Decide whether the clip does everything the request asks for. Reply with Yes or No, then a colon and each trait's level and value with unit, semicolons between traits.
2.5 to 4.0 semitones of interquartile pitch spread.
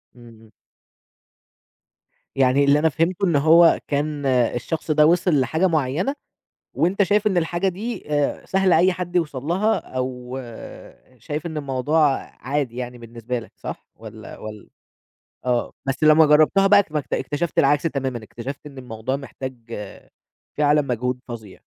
No: average, 4.8 semitones